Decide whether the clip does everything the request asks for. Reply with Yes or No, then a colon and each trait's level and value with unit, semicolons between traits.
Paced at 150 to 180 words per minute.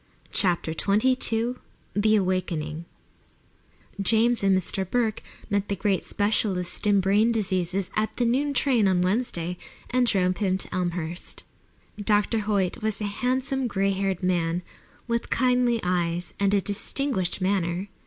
No: slow, 135 wpm